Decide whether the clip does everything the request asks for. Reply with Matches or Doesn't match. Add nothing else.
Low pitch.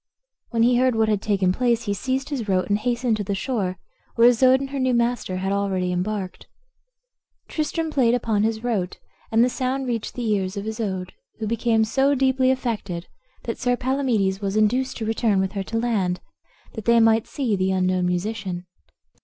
Doesn't match